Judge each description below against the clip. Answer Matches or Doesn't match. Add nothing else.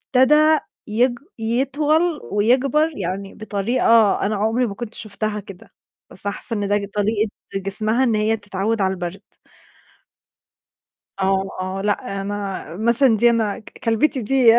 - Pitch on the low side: Doesn't match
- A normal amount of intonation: Matches